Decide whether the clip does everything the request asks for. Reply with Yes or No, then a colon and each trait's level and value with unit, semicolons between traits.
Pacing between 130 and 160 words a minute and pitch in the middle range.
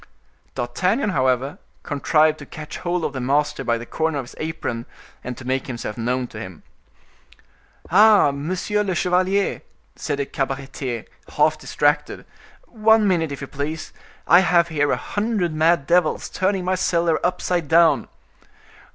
Yes: average, 150 wpm; medium, 155 Hz